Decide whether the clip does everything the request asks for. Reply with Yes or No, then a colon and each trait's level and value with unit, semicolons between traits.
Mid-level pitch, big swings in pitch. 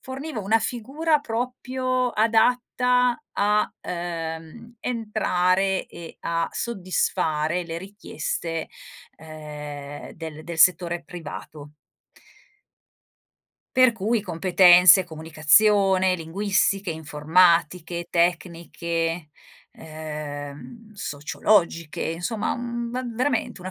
Yes: medium, 180 Hz; wide, 5.7 semitones